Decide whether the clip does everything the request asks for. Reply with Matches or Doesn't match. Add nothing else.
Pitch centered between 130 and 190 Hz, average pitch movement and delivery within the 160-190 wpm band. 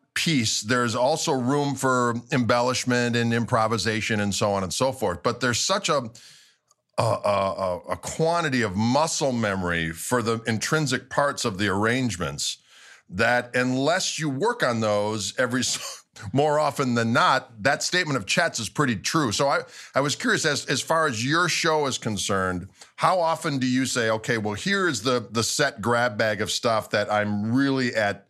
Doesn't match